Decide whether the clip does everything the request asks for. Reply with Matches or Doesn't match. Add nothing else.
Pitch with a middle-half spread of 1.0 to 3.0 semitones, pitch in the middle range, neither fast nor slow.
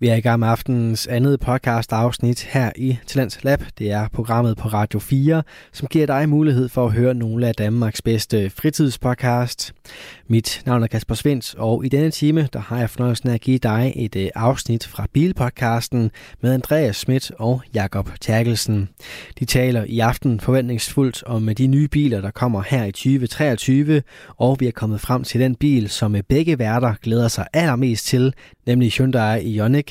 Doesn't match